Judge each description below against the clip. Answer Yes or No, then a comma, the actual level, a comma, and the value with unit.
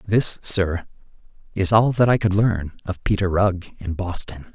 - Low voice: Yes, very low, 95 Hz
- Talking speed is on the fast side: No, average, 170 wpm